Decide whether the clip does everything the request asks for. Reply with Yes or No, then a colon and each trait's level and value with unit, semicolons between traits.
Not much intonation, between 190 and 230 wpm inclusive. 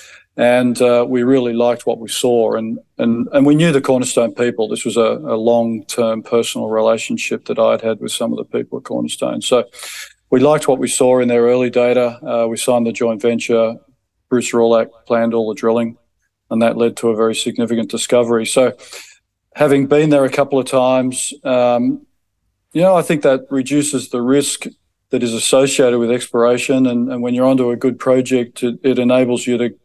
Yes: narrow, 2.1 semitones; average, 200 wpm